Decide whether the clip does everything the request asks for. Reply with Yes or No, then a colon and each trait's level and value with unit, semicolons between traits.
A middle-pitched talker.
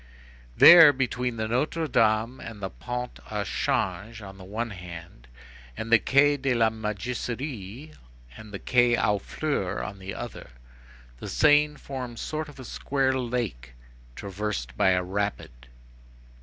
No: low, 115 Hz